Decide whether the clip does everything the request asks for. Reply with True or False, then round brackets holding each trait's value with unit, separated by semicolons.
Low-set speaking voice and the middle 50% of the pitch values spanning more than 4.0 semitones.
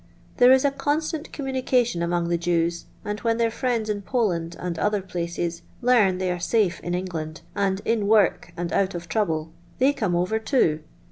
False (195 Hz; 5.3 semitones)